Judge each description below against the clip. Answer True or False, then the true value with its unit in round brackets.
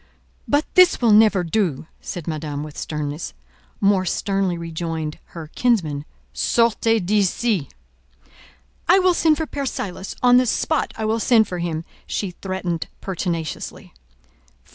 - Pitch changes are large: True (5.8 semitones)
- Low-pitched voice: False (190 Hz)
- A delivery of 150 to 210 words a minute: False (135 wpm)